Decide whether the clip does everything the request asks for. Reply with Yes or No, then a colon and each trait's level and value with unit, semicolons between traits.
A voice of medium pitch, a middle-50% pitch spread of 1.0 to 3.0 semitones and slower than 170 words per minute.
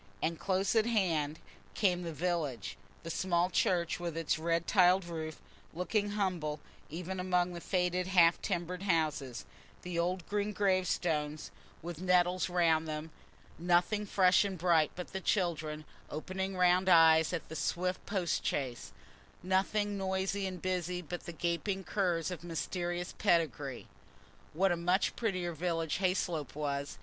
Yes: medium, 175 Hz; narrow, 2.4 semitones; average, 145 wpm